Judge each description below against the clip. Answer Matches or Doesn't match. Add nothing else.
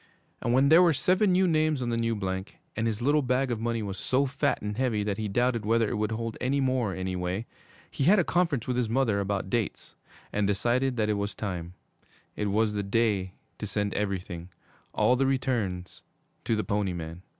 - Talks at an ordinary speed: Doesn't match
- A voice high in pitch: Doesn't match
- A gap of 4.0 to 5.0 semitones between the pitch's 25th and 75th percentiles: Matches